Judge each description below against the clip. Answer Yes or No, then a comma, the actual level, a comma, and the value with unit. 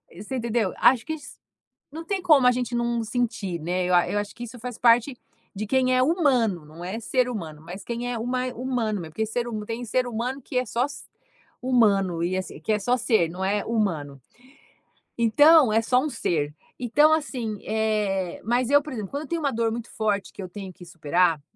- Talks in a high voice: Yes, high, 230 Hz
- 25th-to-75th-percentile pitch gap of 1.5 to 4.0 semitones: No, average, 4.5 semitones